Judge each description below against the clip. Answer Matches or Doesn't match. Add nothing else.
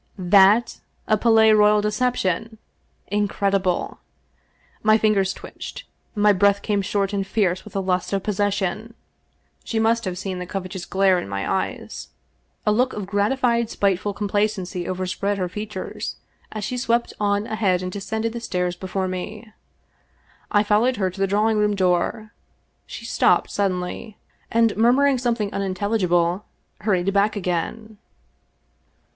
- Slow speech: Doesn't match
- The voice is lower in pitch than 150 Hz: Doesn't match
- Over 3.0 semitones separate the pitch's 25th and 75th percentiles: Doesn't match